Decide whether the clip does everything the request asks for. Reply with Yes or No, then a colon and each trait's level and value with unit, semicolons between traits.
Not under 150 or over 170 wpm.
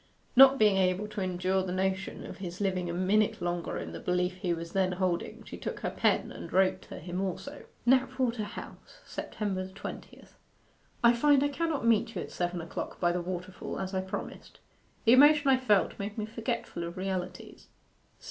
No: average, 185 wpm